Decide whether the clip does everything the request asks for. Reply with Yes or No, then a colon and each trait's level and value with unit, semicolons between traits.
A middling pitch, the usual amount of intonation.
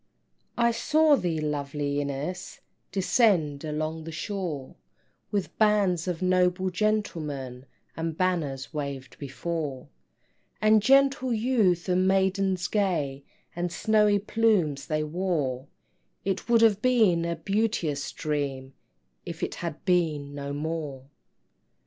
No: medium, 175 Hz; wide, 5.7 semitones